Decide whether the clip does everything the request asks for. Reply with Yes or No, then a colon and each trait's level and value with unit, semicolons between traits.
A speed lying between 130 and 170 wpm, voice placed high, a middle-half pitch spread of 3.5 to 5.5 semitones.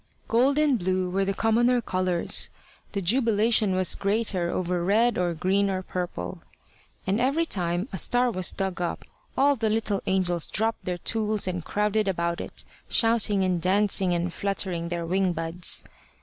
Yes: average, 165 wpm; high, 195 Hz; average, 3.8 semitones